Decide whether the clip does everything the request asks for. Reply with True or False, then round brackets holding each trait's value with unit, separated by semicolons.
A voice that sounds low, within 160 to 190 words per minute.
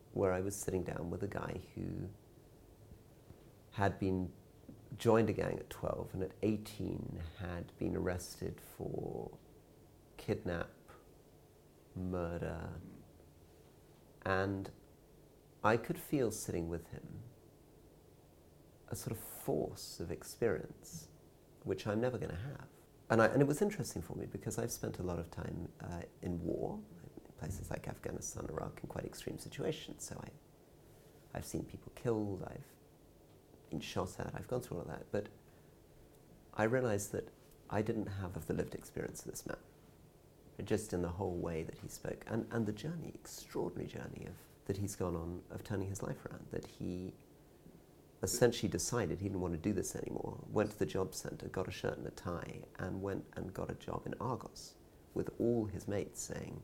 True (100 Hz; 170 wpm)